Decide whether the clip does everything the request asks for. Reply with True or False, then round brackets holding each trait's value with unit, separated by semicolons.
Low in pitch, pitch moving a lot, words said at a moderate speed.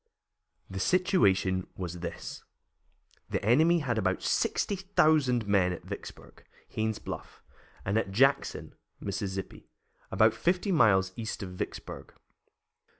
False (110 Hz; 8.0 semitones; 115 wpm)